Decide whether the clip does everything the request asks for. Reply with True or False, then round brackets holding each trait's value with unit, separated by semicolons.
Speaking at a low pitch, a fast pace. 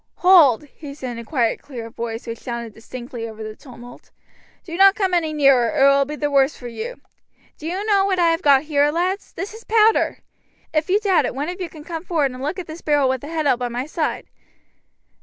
False (295 Hz; 240 wpm)